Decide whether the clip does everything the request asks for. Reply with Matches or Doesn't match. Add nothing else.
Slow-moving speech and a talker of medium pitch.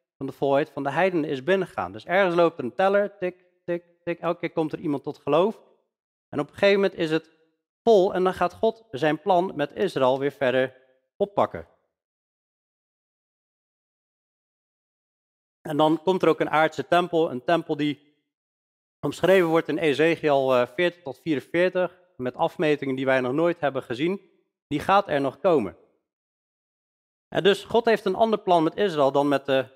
Doesn't match